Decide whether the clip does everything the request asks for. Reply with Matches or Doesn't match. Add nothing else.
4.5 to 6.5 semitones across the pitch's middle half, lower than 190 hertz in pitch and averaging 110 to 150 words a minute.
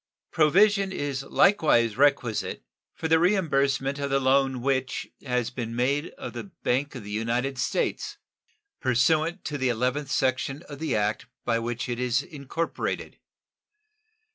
Doesn't match